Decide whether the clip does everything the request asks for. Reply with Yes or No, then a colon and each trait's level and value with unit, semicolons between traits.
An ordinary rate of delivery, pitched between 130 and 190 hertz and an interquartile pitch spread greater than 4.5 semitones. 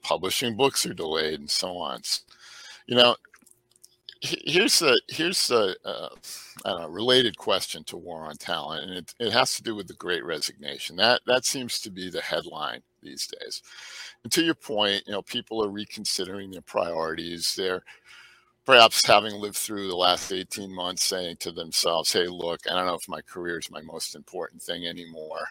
No: average, 180 wpm; low, 100 Hz; average, 5.2 semitones